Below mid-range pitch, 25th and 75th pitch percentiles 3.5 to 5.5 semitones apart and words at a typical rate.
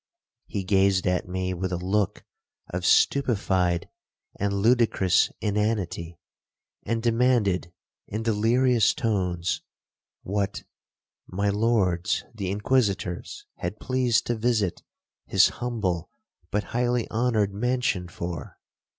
No: low, 100 Hz; average, 4.0 semitones; slow, 105 wpm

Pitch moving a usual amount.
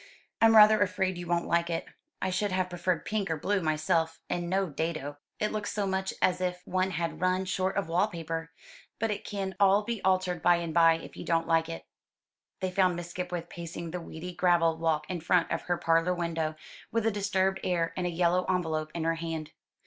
No: narrow, 2.3 semitones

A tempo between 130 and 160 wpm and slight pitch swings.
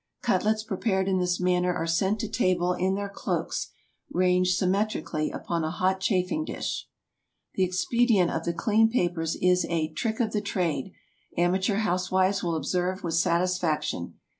Yes: average, 155 wpm; narrow, 2.3 semitones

